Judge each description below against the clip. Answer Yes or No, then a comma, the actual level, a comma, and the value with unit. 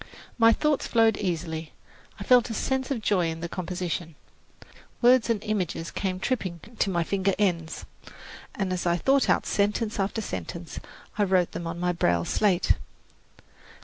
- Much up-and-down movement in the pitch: No, average, 4.3 semitones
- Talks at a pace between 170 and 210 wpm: No, average, 160 wpm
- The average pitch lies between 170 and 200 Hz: Yes, medium, 185 Hz